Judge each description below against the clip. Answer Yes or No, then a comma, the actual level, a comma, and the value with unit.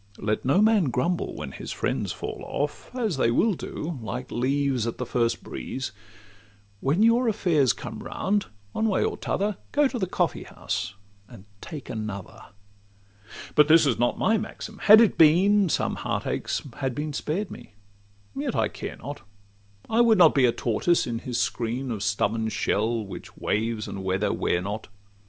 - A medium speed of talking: Yes, average, 180 wpm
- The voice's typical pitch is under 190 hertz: Yes, low, 135 Hz